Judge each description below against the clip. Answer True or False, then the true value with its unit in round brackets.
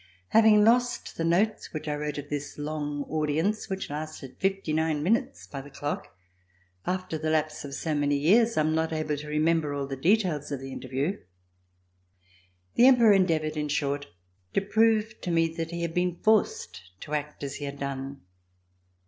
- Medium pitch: True (155 Hz)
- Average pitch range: True (4.6 semitones)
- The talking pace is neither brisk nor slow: True (180 wpm)